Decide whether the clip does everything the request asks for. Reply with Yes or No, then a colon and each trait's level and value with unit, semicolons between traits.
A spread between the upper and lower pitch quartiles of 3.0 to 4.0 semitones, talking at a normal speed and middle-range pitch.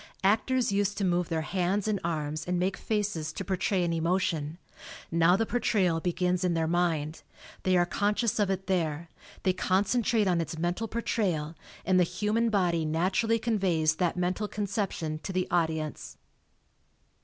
Yes: average, 3.5 semitones; average, 165 wpm; medium, 180 Hz